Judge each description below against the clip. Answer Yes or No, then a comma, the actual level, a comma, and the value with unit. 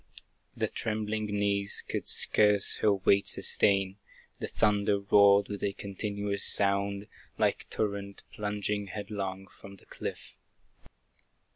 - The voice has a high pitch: No, low, 100 Hz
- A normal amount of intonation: No, narrow, 0.7 semitones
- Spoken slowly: Yes, slow, 115 wpm